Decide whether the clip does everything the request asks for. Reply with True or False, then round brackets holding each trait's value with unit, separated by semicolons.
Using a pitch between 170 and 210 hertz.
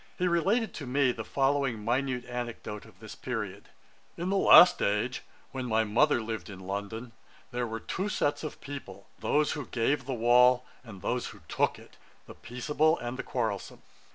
False (125 Hz)